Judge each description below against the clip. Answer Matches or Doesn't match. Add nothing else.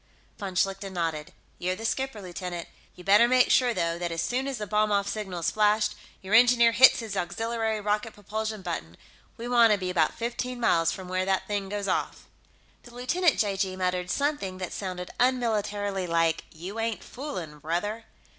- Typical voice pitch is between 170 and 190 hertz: Doesn't match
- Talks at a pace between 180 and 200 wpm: Matches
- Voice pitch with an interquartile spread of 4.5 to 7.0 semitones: Doesn't match